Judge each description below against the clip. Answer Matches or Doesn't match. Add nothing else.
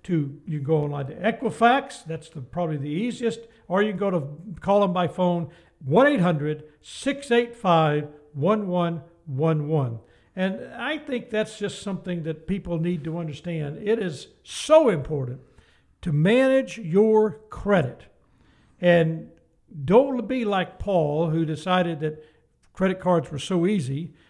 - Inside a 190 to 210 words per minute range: Doesn't match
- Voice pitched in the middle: Matches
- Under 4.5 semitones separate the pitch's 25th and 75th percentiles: Doesn't match